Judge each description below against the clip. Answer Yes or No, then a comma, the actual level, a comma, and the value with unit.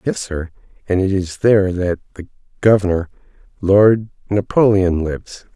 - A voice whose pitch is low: Yes, very low, 95 Hz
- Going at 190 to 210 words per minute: No, average, 140 wpm